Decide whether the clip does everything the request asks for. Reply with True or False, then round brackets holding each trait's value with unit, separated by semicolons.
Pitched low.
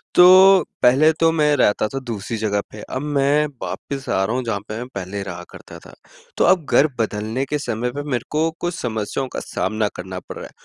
True (125 Hz)